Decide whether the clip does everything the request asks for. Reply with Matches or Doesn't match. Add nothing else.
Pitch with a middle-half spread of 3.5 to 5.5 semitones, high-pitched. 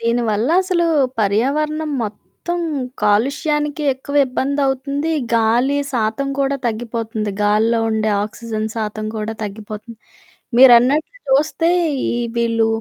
Matches